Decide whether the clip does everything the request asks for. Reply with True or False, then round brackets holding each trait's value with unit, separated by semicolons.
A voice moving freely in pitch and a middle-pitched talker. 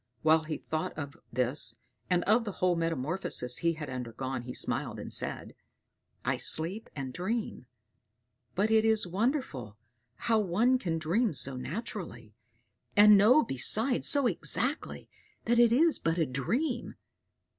True (8.3 semitones; 175 Hz)